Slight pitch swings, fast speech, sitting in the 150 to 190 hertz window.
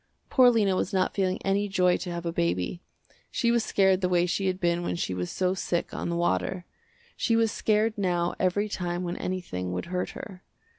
Yes: narrow, 2.2 semitones; fast, 210 wpm; medium, 185 Hz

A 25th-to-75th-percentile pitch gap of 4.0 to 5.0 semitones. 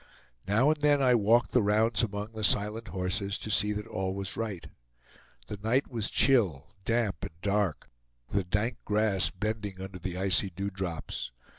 No: average, 2.9 semitones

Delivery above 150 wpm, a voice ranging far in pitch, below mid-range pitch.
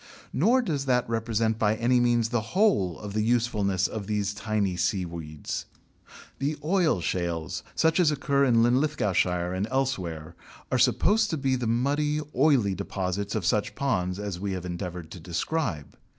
Yes: average, 160 wpm; wide, 6.7 semitones; low, 110 Hz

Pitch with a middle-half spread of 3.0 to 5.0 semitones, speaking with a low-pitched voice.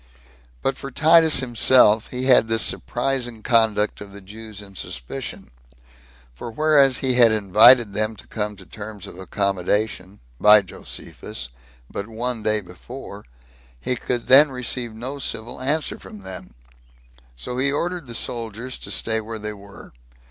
Yes: average, 3.6 semitones; low, 110 Hz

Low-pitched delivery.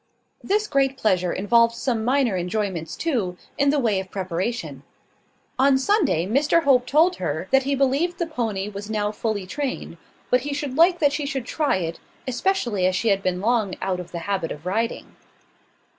No: high, 235 Hz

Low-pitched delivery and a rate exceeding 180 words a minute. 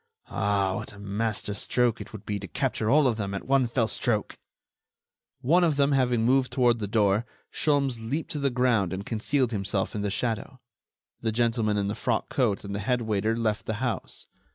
Yes: low, 115 Hz; average, 200 wpm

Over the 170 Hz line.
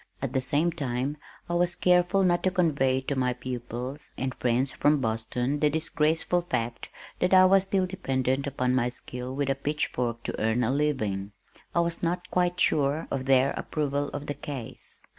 No: medium, 140 Hz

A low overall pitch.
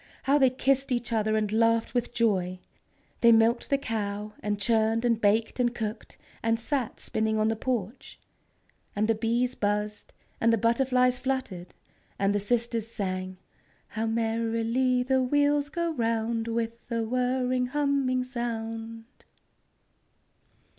No: high, 230 Hz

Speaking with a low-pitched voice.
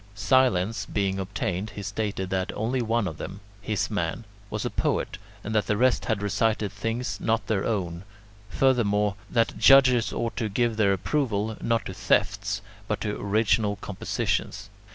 Yes: low, 105 Hz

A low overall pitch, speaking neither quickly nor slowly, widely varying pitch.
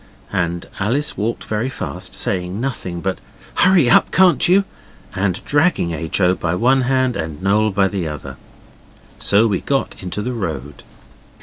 Yes: low, 100 Hz; average, 160 wpm; wide, 6.4 semitones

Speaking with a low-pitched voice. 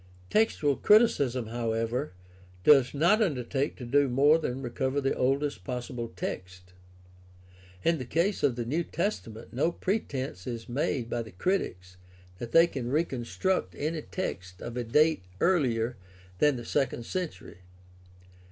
Yes: low, 130 Hz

